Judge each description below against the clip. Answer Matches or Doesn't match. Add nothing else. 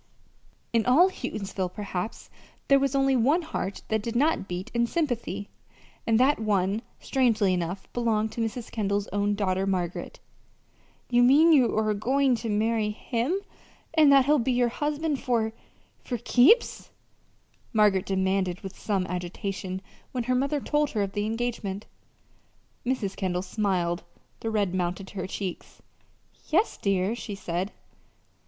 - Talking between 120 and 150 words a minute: Matches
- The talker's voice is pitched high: Matches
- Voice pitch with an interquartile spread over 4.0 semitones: Matches